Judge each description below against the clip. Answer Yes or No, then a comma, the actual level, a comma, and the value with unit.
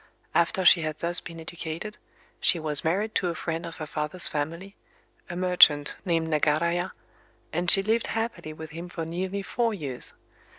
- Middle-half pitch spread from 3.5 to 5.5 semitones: No, average, 2.9 semitones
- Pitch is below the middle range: No, medium, 170 Hz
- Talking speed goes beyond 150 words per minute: Yes, average, 160 wpm